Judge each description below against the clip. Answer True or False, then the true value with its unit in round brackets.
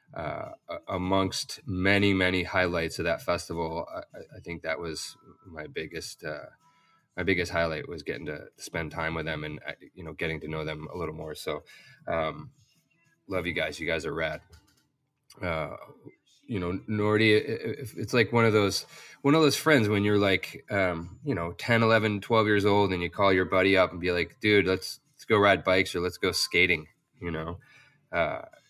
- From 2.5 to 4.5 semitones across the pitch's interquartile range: False (5.3 semitones)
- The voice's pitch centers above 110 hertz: False (100 Hz)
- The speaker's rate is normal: True (190 wpm)